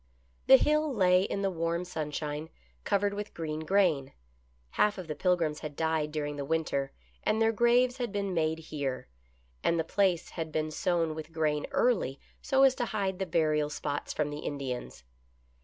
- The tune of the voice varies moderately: Yes, average, 4.7 semitones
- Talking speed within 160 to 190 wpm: Yes, average, 175 wpm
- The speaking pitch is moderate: Yes, medium, 165 Hz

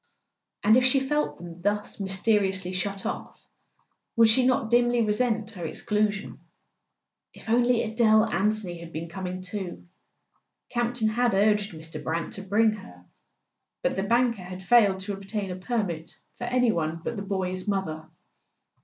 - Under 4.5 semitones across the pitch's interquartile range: Yes, average, 3.7 semitones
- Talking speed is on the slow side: No, average, 155 wpm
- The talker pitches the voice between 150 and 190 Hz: No, high, 205 Hz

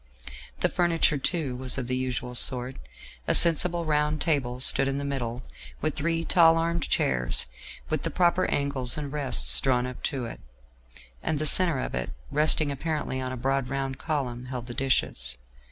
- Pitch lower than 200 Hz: Yes, low, 135 Hz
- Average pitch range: Yes, average, 3.6 semitones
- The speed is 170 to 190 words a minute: Yes, average, 175 wpm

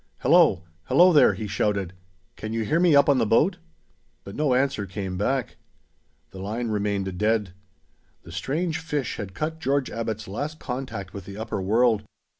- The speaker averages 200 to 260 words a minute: No, average, 170 wpm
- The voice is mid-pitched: No, low, 115 Hz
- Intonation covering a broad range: Yes, wide, 6.0 semitones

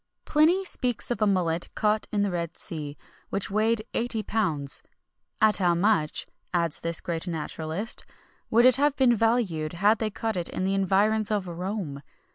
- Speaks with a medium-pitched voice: No, high, 200 Hz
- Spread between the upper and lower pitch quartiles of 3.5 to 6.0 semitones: Yes, average, 4.7 semitones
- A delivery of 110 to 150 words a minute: No, average, 175 wpm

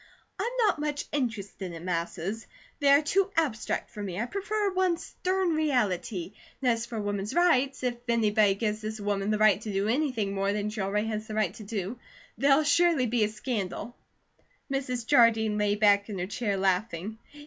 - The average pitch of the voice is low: No, high, 220 Hz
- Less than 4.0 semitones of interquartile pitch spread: No, average, 5.1 semitones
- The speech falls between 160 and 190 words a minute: Yes, average, 185 wpm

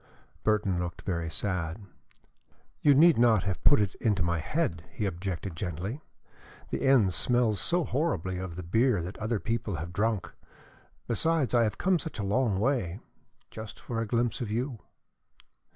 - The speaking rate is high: No, average, 165 wpm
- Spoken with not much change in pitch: No, average, 5.0 semitones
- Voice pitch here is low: Yes, low, 105 Hz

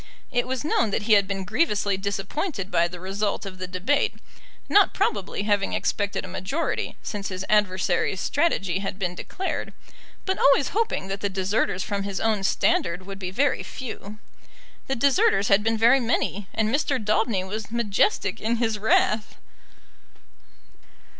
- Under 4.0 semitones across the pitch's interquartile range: Yes, average, 3.5 semitones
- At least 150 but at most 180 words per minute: Yes, average, 160 wpm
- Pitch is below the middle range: No, high, 205 Hz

